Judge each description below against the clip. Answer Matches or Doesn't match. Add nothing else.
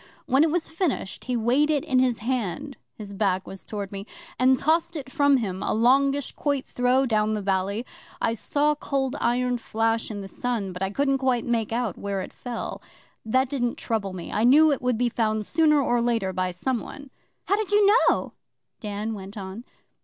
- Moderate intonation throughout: Matches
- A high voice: Matches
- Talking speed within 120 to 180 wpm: Doesn't match